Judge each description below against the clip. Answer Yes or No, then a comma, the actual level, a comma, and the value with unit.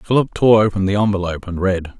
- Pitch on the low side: Yes, low, 100 Hz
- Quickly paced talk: Yes, fast, 210 wpm